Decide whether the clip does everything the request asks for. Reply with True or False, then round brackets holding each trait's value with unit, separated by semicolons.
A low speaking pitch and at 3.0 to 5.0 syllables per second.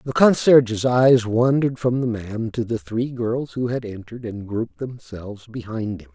True (120 Hz; 4.8 syllables/s)